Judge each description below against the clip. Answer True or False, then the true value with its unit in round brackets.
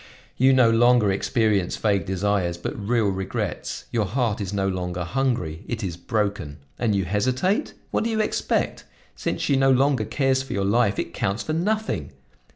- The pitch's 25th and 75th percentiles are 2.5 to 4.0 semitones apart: False (5.0 semitones)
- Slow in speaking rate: False (175 wpm)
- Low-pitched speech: True (110 Hz)